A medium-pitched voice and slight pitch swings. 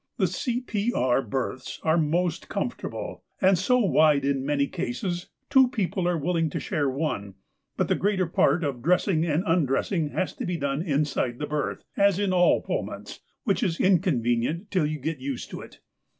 No: medium, 165 Hz; average, 4.9 semitones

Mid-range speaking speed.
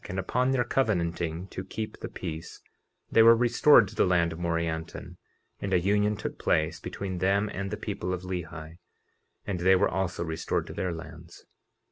Yes: average, 180 wpm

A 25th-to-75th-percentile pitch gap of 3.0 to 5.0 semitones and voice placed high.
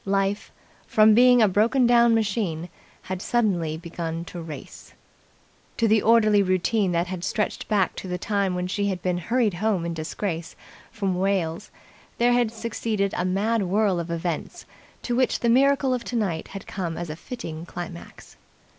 Yes: average, 4.4 semitones; high, 195 Hz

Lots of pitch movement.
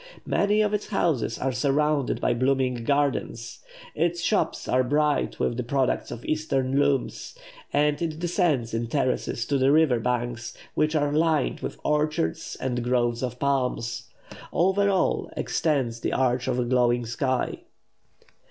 No: average, 3.8 semitones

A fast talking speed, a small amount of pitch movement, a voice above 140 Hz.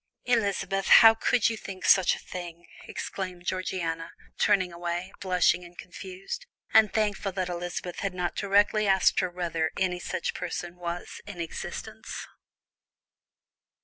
No: slow, 135 wpm; narrow, 2.1 semitones; medium, 185 Hz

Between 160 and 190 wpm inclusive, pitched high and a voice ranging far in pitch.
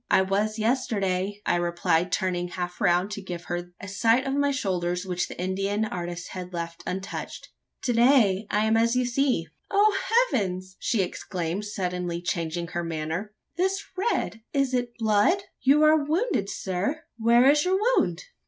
Yes: average, 165 wpm; high, 200 Hz; wide, 6.0 semitones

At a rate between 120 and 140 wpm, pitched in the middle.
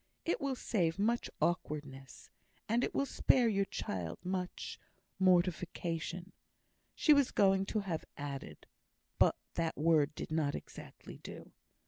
Yes: slow, 135 wpm; medium, 180 Hz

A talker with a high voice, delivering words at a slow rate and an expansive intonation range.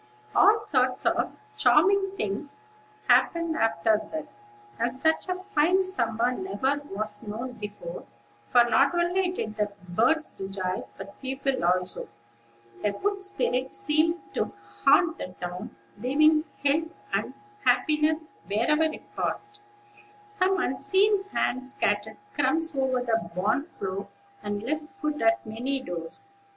Yes: very high, 270 Hz; slow, 130 wpm; wide, 7.6 semitones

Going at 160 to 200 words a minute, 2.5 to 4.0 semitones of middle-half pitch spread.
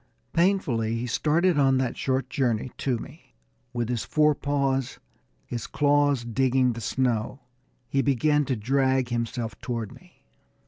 No: slow, 135 wpm; average, 3.1 semitones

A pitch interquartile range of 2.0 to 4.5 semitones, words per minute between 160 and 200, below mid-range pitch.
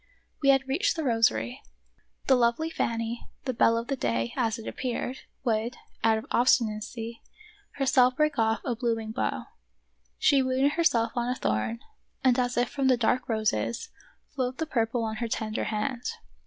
No: narrow, 2.6 semitones; average, 170 wpm; high, 240 Hz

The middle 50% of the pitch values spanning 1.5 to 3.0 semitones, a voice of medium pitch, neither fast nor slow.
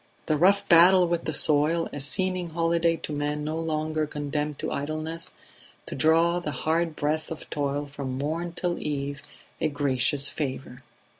Yes: narrow, 2.4 semitones; medium, 155 Hz; average, 160 wpm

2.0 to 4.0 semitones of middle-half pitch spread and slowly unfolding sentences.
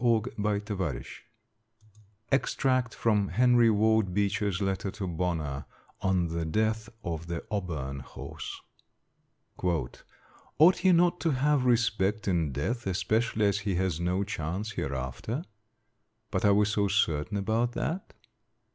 No: average, 4.7 semitones; slow, 120 wpm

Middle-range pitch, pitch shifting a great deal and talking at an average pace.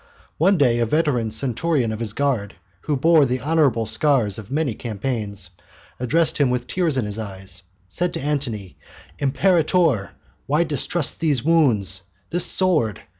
No: low, 130 Hz; wide, 6.0 semitones; average, 150 wpm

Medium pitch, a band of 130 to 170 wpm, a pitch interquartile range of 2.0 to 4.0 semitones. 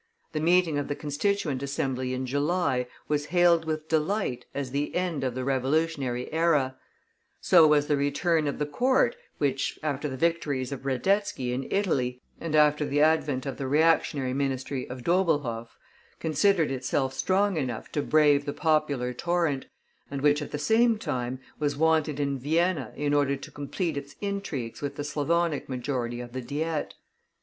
Yes: medium, 145 Hz; average, 165 wpm; average, 3.4 semitones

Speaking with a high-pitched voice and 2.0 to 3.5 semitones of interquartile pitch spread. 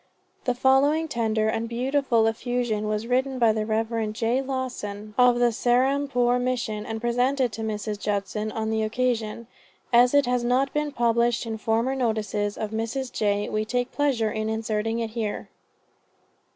Yes: high, 230 Hz; narrow, 2.4 semitones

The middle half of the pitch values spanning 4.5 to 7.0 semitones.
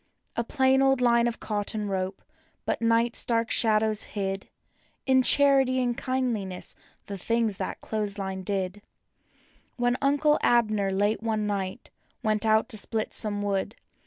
No: average, 3.1 semitones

